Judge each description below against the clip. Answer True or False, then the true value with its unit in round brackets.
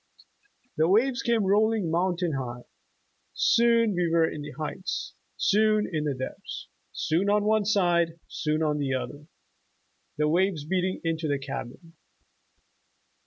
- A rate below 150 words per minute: True (135 wpm)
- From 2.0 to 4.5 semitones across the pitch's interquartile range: False (5.2 semitones)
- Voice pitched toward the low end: False (170 Hz)